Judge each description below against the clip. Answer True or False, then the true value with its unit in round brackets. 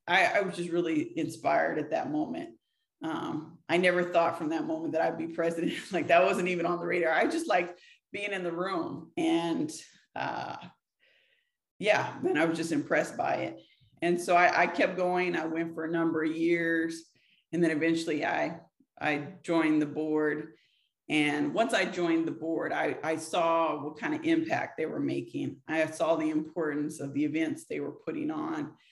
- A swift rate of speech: False (190 wpm)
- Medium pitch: True (170 Hz)